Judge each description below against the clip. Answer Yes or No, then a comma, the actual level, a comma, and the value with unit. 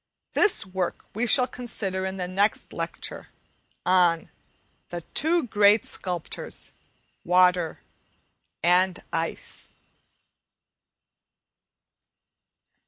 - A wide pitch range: No, average, 3.1 semitones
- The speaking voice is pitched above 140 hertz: Yes, medium, 185 Hz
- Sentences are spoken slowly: Yes, slow, 80 wpm